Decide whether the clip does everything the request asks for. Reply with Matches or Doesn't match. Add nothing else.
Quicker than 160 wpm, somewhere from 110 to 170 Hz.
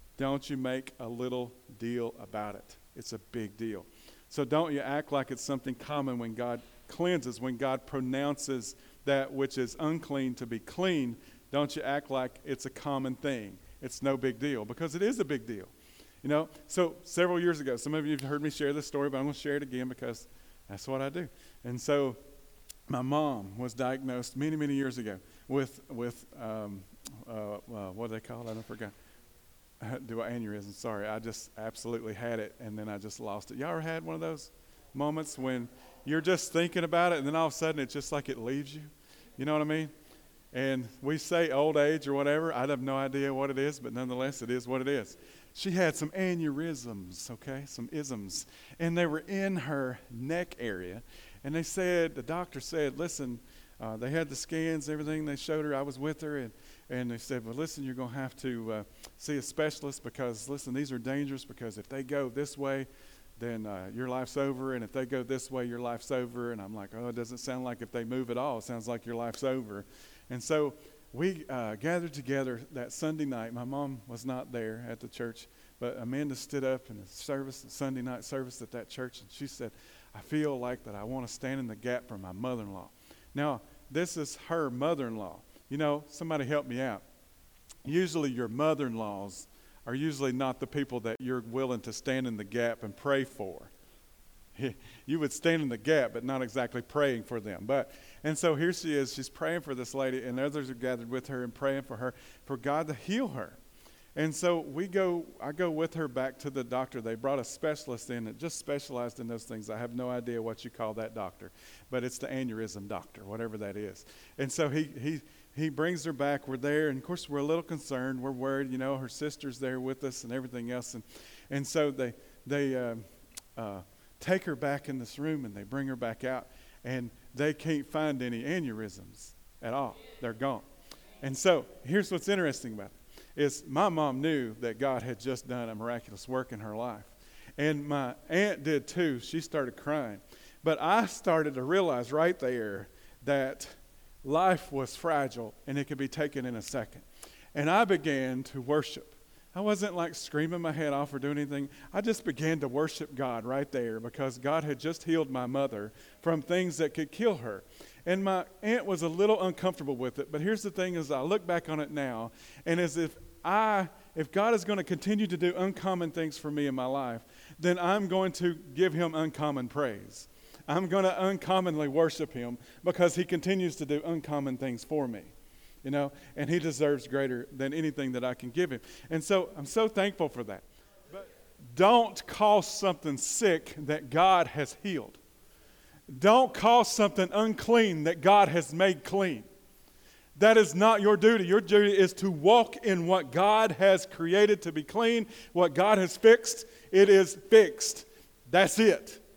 Matches